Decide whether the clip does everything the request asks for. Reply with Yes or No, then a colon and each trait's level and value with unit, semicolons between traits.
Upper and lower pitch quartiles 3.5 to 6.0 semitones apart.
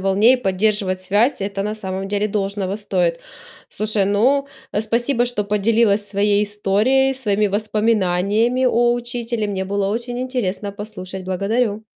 No: average, 3.0 semitones